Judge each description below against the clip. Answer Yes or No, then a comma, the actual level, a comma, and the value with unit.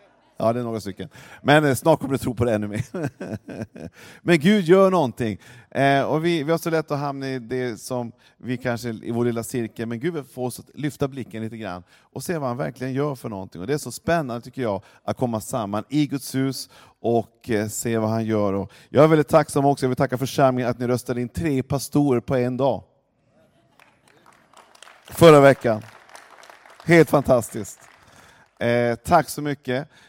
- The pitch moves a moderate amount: Yes, average, 3.8 semitones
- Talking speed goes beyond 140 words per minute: Yes, fast, 195 wpm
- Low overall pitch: Yes, low, 125 Hz